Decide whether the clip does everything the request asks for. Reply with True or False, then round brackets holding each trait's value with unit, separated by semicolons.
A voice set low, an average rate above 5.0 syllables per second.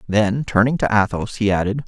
True (105 Hz; 5.3 syllables/s)